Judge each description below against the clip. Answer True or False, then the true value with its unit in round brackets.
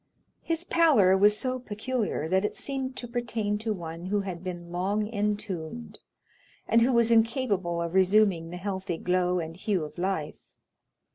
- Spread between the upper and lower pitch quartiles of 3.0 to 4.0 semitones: False (4.5 semitones)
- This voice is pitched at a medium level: False (200 Hz)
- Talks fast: False (160 wpm)